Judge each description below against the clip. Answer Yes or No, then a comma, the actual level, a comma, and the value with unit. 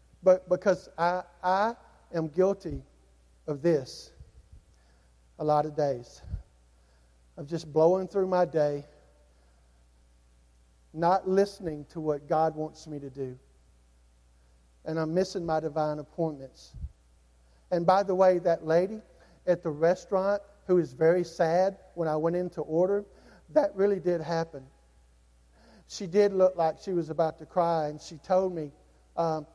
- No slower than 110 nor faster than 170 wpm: Yes, average, 140 wpm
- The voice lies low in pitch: No, medium, 160 Hz